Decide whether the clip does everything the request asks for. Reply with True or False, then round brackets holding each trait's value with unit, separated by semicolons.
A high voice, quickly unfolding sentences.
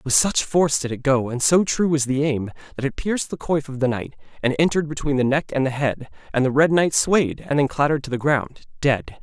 False (140 Hz; 260 wpm)